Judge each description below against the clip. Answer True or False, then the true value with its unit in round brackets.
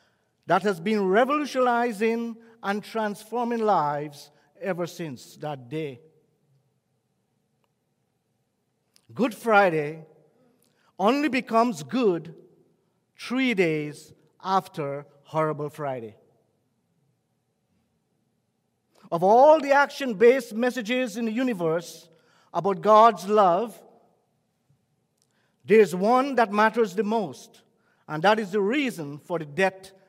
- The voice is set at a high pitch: True (200 Hz)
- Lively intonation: True (6.7 semitones)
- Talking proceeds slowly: True (95 wpm)